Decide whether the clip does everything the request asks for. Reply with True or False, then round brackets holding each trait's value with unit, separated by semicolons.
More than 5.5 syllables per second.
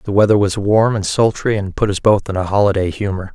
True (5.9 syllables/s)